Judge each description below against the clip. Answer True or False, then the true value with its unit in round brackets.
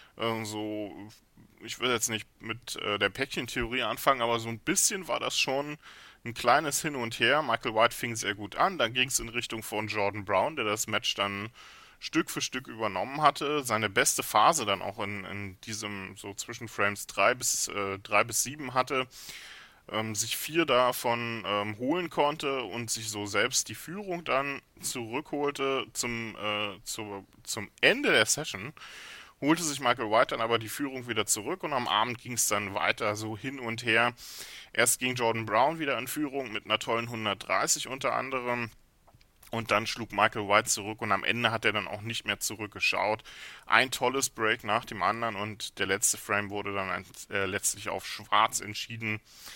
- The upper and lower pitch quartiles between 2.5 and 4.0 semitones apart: True (3.4 semitones)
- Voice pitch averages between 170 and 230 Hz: False (115 Hz)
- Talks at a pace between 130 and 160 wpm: False (180 wpm)